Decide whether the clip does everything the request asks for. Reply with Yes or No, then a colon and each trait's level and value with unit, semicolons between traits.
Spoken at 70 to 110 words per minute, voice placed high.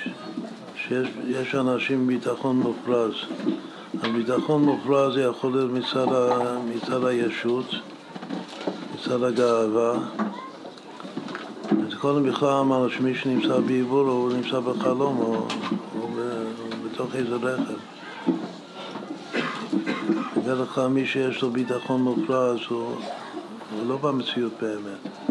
No: slow, 100 wpm; low, 125 Hz